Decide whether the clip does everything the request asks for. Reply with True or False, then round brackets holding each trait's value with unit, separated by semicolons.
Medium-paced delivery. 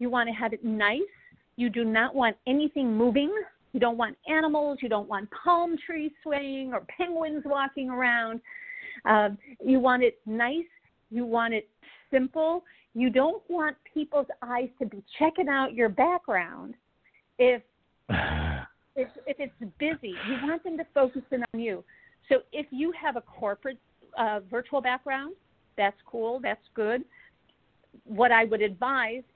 True (155 wpm)